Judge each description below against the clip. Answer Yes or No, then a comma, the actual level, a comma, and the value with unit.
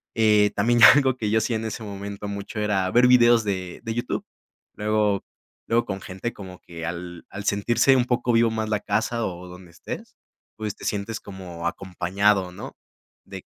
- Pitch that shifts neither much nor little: Yes, average, 3.2 semitones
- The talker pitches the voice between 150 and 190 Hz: No, low, 105 Hz